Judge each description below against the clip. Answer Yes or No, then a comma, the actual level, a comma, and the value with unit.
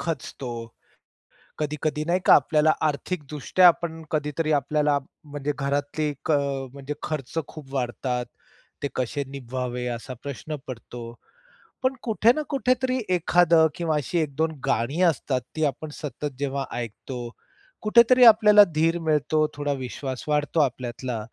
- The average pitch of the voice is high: No, medium, 150 Hz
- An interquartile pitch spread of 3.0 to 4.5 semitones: Yes, average, 3.3 semitones